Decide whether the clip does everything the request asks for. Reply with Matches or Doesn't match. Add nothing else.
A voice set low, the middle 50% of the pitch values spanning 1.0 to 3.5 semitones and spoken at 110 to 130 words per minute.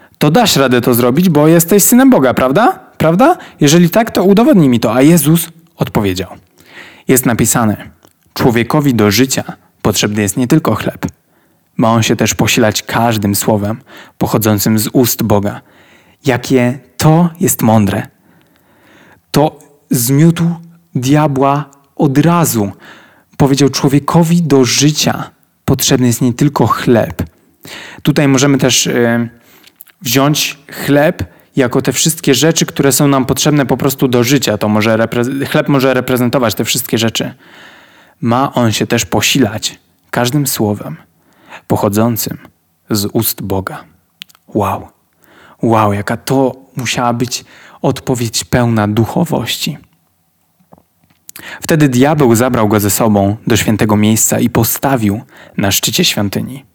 Doesn't match